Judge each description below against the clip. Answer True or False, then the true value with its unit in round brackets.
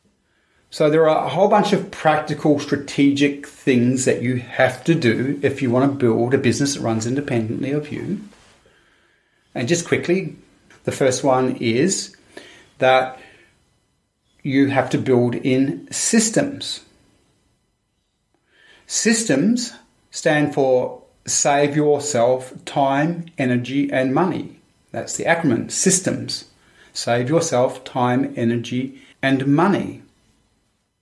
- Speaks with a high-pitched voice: False (135 Hz)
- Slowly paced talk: True (115 wpm)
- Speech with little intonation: False (3.3 semitones)